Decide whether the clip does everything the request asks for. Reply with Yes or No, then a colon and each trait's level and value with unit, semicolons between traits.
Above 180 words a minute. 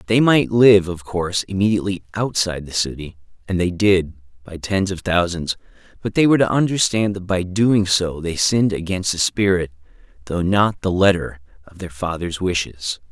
No: average, 175 wpm